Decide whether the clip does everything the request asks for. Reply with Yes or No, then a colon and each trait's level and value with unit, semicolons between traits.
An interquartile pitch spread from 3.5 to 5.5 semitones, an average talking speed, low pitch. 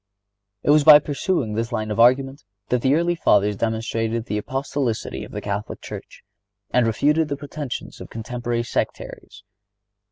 Yes: average, 4.3 semitones; average, 155 wpm; low, 120 Hz